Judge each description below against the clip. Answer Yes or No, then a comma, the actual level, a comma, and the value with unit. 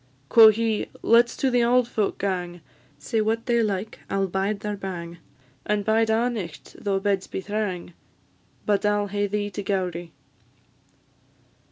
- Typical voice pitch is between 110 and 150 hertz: No, high, 205 Hz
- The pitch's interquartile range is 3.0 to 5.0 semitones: No, narrow, 2.5 semitones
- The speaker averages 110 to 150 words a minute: No, average, 170 wpm